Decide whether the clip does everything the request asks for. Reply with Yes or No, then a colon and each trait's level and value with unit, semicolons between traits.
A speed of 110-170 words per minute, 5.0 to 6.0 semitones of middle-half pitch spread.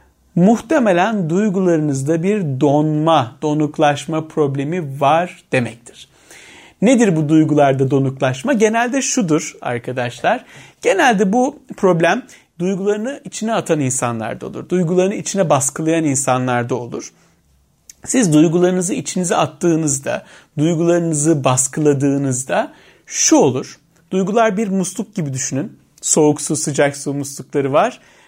No: average, 100 wpm; average, 5.3 semitones